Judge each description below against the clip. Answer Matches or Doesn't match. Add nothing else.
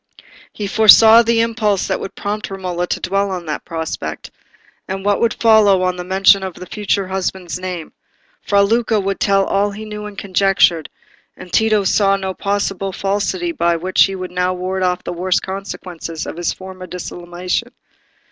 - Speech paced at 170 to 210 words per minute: Matches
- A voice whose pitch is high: Matches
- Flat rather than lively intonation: Matches